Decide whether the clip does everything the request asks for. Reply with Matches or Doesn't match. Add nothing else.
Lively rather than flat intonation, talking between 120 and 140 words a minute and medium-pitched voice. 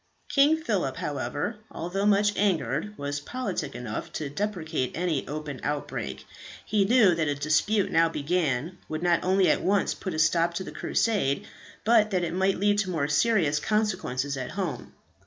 Doesn't match